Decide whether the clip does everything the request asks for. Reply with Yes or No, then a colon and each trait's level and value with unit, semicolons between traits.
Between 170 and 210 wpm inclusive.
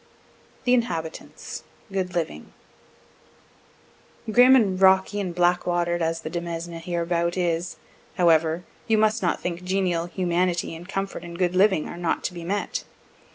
No: average, 145 wpm